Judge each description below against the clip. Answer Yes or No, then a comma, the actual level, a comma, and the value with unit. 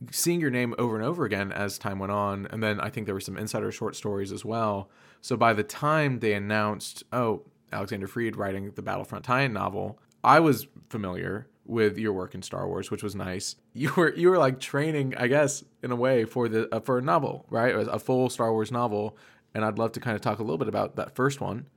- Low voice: Yes, low, 110 Hz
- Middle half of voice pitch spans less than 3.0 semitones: No, average, 3.4 semitones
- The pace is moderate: No, fast, 245 wpm